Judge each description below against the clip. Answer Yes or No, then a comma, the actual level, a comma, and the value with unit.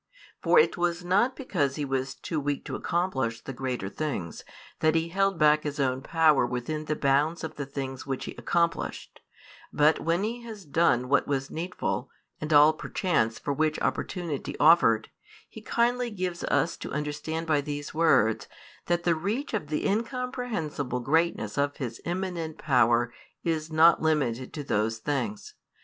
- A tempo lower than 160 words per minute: No, average, 165 wpm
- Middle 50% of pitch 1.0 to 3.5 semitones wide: No, average, 4.2 semitones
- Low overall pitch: No, medium, 155 Hz